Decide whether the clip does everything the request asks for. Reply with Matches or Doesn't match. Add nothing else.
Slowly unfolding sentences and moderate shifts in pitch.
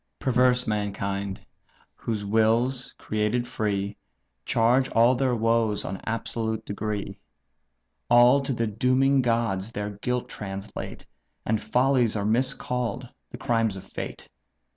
Matches